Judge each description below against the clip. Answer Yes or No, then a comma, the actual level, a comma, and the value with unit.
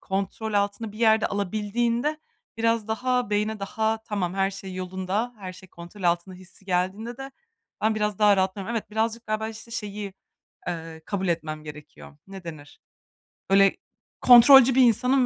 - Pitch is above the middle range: Yes, high, 205 Hz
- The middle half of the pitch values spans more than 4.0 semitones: No, average, 3.2 semitones